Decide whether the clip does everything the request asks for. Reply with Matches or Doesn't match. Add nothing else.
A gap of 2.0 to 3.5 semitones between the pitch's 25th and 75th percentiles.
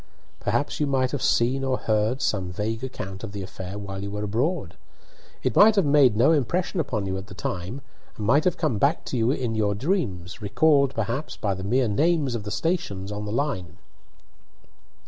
Doesn't match